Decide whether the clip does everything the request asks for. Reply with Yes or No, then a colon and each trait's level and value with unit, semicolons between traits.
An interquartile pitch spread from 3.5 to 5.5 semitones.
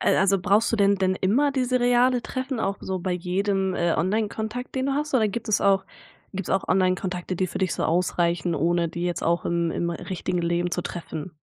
Yes: average, 4.0 semitones